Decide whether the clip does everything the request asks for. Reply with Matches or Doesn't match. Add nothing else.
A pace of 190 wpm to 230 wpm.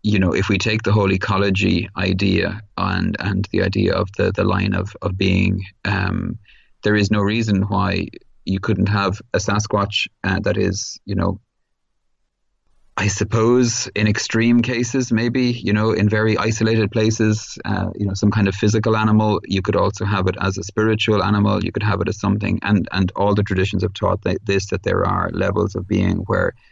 Matches